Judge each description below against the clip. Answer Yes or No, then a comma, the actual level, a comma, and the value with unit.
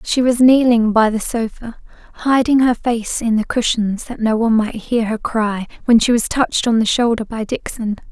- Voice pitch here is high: Yes, high, 230 Hz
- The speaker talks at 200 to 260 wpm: Yes, fast, 205 wpm